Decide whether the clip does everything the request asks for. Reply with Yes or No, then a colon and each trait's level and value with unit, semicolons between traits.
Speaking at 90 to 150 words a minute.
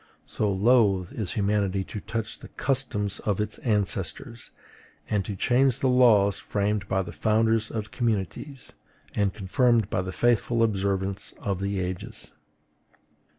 Yes: average, 140 wpm